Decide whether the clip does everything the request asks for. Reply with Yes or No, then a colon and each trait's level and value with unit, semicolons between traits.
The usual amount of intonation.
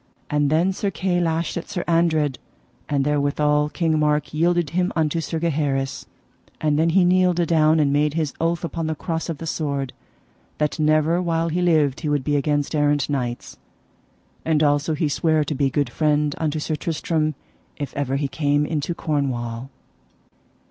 No: narrow, 2.2 semitones